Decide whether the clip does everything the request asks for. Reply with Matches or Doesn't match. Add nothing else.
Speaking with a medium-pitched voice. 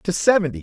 Matches